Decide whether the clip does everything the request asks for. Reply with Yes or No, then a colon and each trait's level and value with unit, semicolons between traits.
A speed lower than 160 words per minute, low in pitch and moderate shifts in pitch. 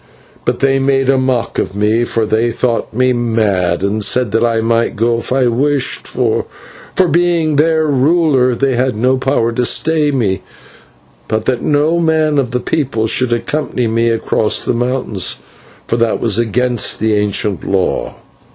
No: average, 170 wpm; low, 120 Hz; average, 3.3 semitones